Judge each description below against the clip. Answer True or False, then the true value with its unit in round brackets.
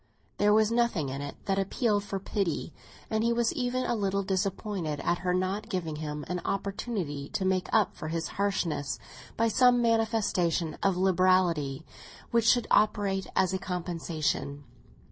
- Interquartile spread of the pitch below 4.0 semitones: False (4.3 semitones)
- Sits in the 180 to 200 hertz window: True (190 Hz)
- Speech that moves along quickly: False (160 wpm)